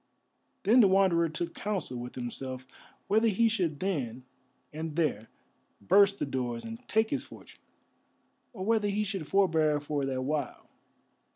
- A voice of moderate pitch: Yes, medium, 165 Hz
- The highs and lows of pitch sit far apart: Yes, wide, 7.0 semitones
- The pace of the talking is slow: No, average, 150 wpm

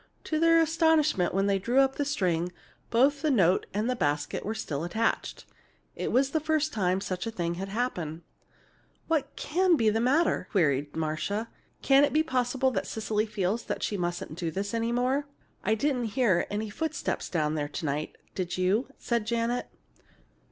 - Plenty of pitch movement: Yes, wide, 7.0 semitones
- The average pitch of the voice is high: Yes, high, 220 Hz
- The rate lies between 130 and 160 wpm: No, average, 175 wpm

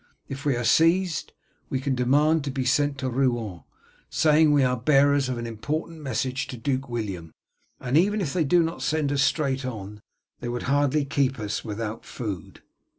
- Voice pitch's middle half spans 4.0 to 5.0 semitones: No, average, 3.6 semitones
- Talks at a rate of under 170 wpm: No, average, 185 wpm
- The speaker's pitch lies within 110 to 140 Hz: Yes, low, 135 Hz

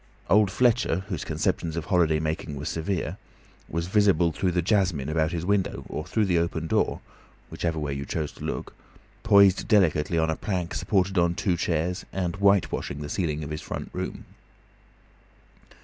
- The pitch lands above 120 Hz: No, very low, 85 Hz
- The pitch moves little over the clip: No, average, 3.5 semitones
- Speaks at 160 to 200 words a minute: Yes, average, 170 wpm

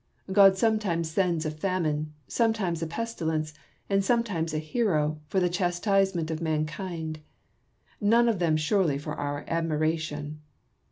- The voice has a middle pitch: Yes, medium, 165 Hz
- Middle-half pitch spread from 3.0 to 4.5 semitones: Yes, average, 3.9 semitones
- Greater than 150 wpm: No, slow, 135 wpm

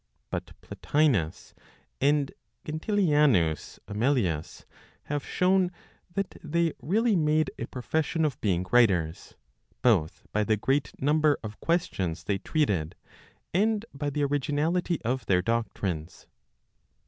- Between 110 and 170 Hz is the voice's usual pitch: Yes, medium, 140 Hz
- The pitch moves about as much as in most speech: No, wide, 7.5 semitones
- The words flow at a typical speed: No, slow, 110 wpm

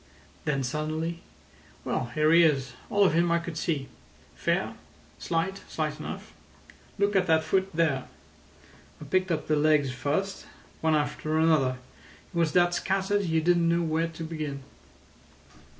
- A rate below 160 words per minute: Yes, average, 145 wpm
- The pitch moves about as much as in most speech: No, narrow, 2.2 semitones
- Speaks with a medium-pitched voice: Yes, medium, 160 Hz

